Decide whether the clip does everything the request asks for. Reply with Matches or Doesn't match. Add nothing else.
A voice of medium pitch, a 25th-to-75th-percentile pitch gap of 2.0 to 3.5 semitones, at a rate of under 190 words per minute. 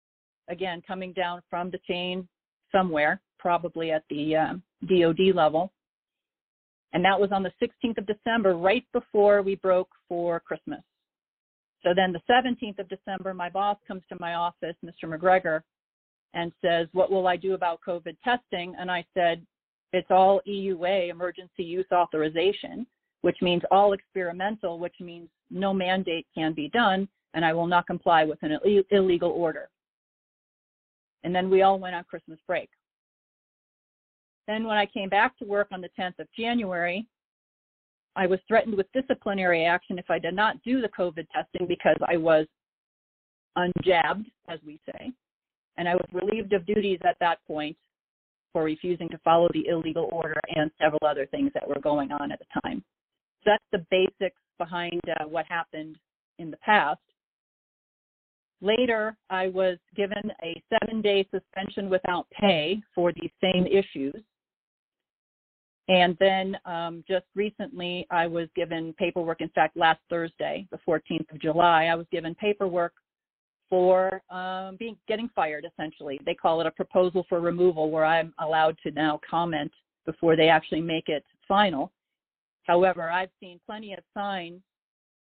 Matches